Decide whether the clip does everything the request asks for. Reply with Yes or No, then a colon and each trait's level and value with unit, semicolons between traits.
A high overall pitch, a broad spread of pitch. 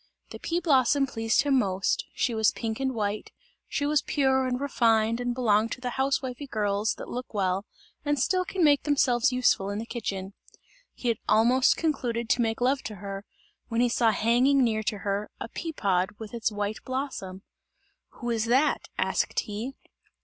No: high, 235 Hz; average, 3.8 semitones